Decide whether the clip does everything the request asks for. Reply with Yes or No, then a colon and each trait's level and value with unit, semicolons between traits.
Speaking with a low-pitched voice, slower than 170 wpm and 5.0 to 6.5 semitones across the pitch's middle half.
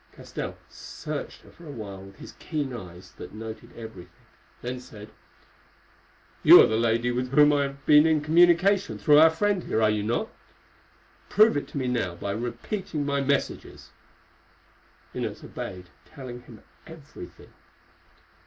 Yes: low, 125 Hz; average, 155 wpm; wide, 5.5 semitones